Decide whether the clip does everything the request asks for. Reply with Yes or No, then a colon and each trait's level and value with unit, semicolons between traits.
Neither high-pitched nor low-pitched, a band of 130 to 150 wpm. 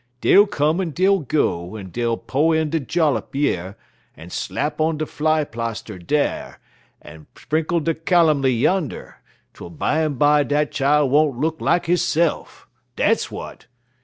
Yes: medium, 150 Hz; average, 145 wpm